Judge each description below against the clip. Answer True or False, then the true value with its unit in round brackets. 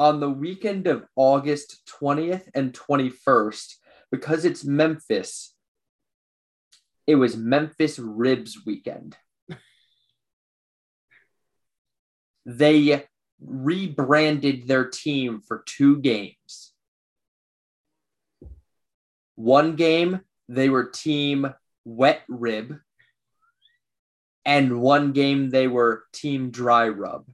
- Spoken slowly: True (85 wpm)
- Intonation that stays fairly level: False (3.9 semitones)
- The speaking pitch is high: False (135 Hz)